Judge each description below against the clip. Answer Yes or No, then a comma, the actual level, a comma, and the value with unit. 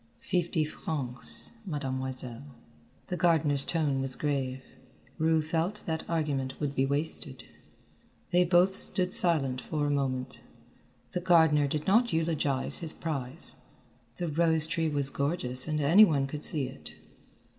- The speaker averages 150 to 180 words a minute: No, slow, 135 wpm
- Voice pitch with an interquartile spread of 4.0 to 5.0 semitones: No, average, 3.5 semitones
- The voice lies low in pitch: No, medium, 150 Hz